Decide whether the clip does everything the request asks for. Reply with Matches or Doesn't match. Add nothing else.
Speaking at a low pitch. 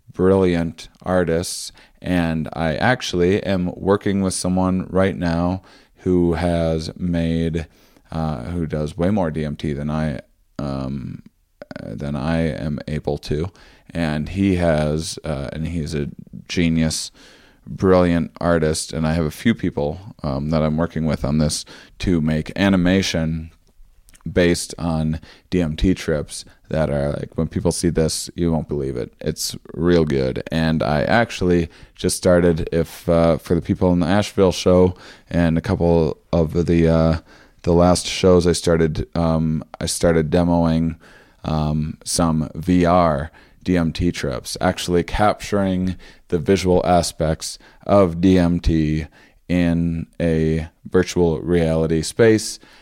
Matches